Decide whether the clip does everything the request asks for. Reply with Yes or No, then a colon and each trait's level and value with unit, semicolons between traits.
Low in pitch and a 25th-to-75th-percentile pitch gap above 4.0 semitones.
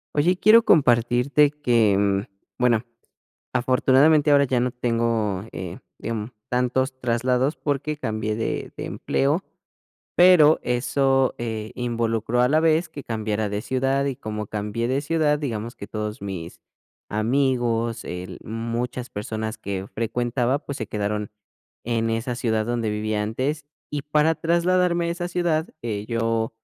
Yes: low, 120 Hz; average, 4.5 semitones